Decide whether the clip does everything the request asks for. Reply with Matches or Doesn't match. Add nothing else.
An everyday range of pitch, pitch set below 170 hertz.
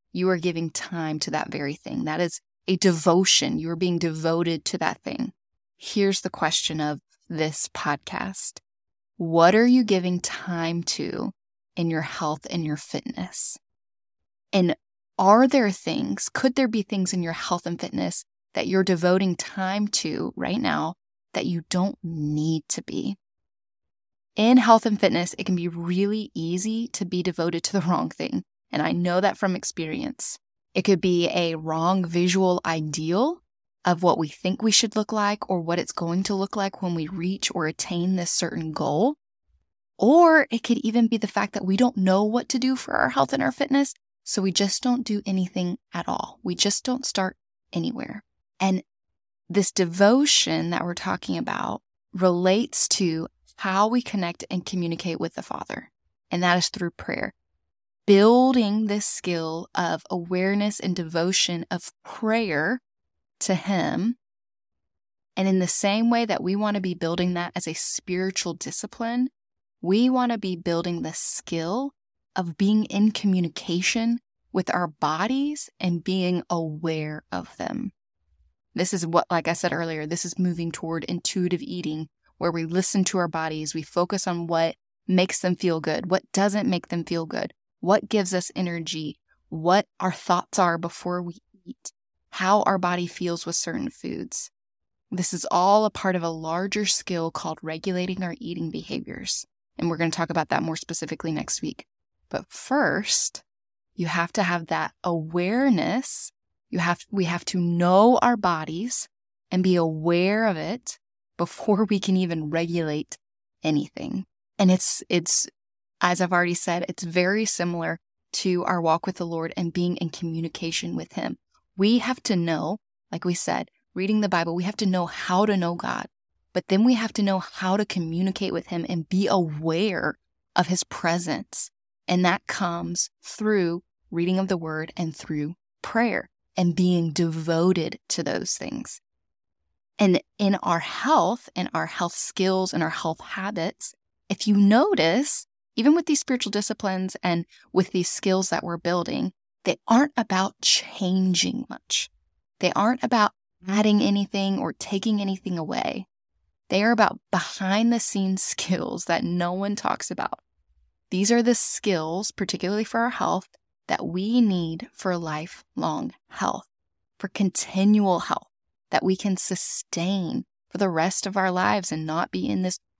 Doesn't match